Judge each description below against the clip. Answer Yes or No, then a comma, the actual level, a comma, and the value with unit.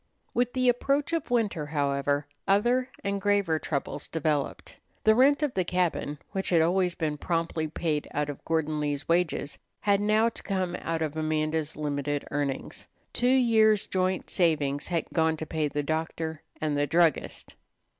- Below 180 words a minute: Yes, average, 165 wpm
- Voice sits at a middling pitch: Yes, medium, 165 Hz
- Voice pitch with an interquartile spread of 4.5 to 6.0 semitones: Yes, average, 5.1 semitones